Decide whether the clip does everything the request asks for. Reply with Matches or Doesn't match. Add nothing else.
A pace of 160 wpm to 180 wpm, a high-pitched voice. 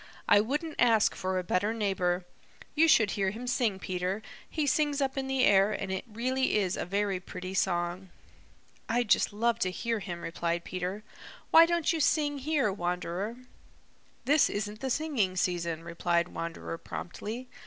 Matches